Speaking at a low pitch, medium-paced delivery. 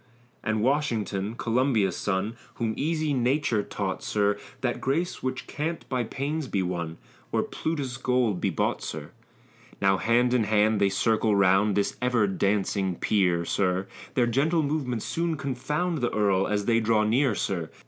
Yes: low, 115 Hz; average, 160 wpm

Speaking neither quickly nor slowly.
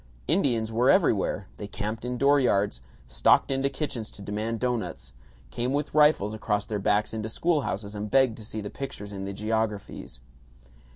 Yes: average, 165 wpm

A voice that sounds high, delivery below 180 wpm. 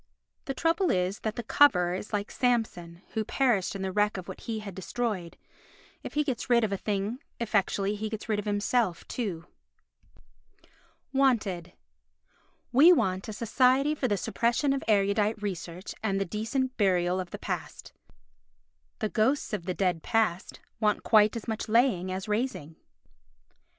Yes: high, 210 Hz; average, 160 wpm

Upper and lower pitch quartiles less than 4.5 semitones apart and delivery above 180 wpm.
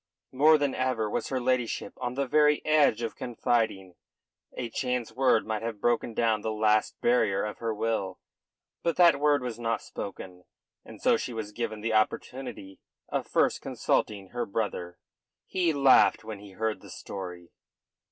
No: average, 3.3 semitones; average, 165 wpm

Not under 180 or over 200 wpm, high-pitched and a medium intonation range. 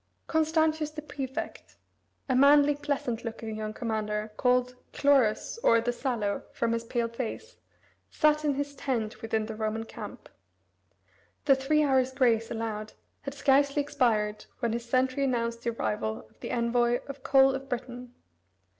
No: average, 150 wpm; very high, 250 Hz; average, 3.6 semitones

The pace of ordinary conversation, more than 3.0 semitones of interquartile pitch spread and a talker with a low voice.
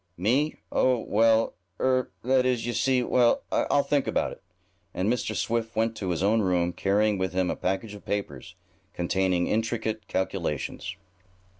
Yes: average, 160 wpm; average, 4.3 semitones; low, 110 Hz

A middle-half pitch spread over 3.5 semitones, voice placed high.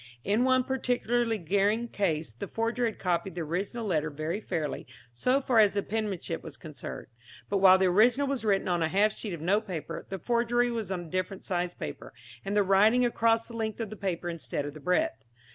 Yes: average, 4.6 semitones; high, 200 Hz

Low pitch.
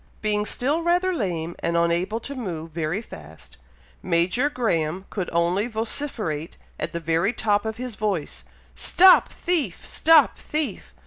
No: high, 205 Hz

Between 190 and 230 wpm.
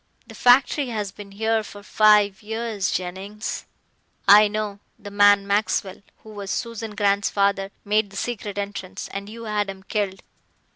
No: average, 160 wpm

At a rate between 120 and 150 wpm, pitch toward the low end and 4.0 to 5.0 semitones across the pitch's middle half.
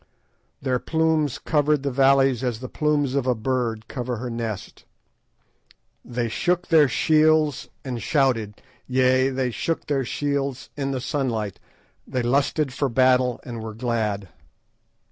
No: average, 140 wpm; low, 130 Hz; average, 3.0 semitones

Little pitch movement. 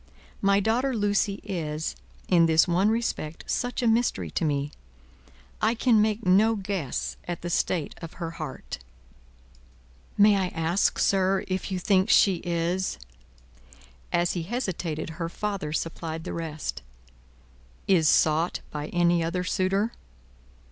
No: average, 3.8 semitones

